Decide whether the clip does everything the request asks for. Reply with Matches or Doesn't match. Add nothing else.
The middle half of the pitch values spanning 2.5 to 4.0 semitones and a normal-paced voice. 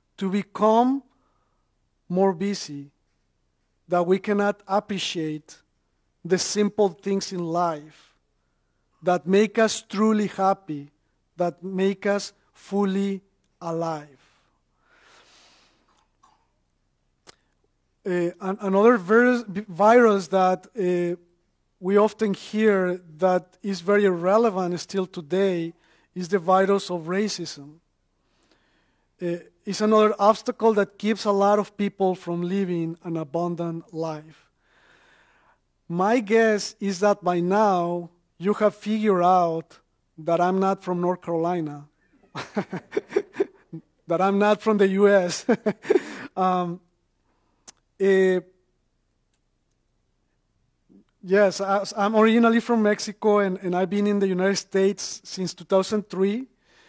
Doesn't match